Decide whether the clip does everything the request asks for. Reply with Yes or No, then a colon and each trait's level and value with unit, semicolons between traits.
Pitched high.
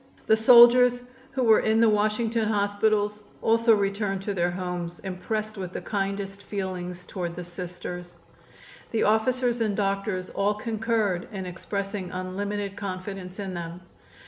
Yes: high, 200 Hz